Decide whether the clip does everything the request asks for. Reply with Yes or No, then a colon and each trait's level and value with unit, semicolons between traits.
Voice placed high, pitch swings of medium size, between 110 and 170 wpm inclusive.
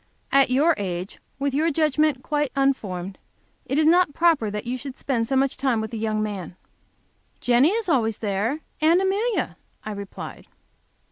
No: very high, 265 Hz; wide, 6.2 semitones; average, 165 wpm